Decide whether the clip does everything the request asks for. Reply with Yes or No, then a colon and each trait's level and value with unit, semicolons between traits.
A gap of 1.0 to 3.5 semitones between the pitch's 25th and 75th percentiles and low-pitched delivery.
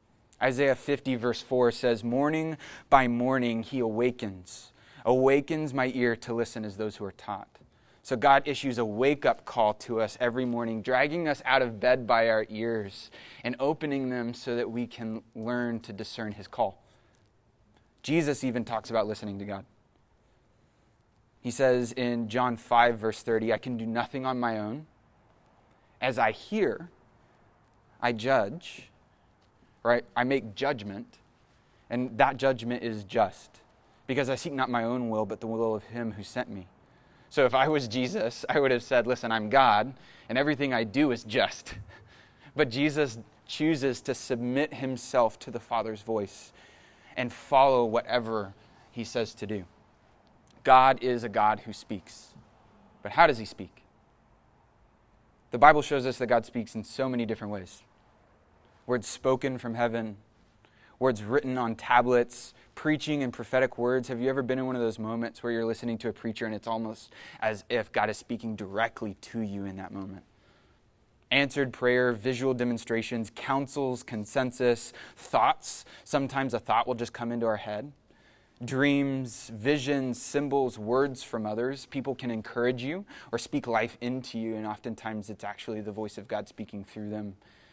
Yes: average, 2.8 semitones; low, 120 Hz